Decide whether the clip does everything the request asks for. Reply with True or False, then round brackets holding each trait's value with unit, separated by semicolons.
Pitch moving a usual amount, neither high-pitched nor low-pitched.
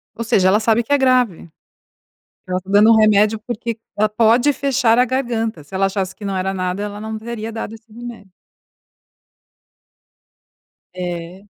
False (3.3 semitones; 215 Hz)